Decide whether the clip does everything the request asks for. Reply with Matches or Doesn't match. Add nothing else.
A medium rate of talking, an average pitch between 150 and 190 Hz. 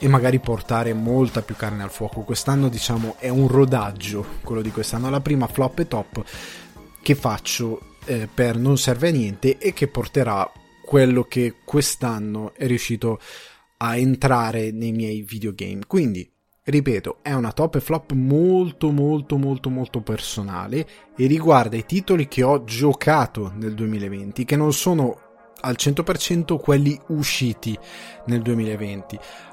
Doesn't match